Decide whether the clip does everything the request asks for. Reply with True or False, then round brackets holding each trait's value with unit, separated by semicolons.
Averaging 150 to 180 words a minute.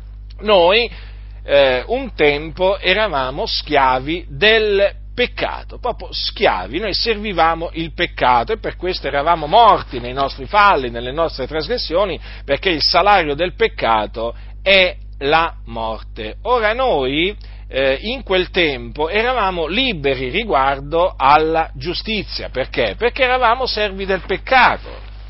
False (120 wpm)